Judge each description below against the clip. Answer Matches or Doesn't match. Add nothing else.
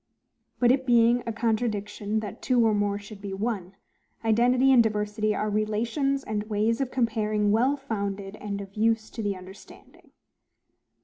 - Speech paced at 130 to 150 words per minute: Doesn't match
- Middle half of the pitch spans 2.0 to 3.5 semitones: Matches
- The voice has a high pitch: Matches